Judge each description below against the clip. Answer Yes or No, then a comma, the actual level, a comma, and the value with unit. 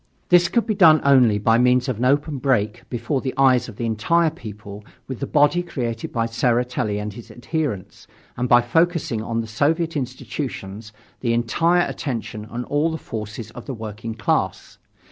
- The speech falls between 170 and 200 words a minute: Yes, average, 180 wpm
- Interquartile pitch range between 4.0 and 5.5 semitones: Yes, average, 4.4 semitones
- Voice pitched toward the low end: Yes, low, 120 Hz